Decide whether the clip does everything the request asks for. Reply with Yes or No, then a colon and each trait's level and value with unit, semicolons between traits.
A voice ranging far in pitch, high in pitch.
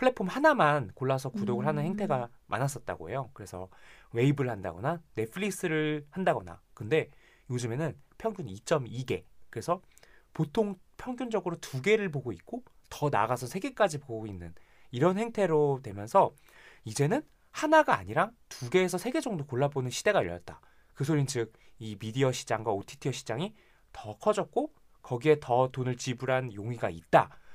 No: wide, 7.5 semitones; medium, 140 Hz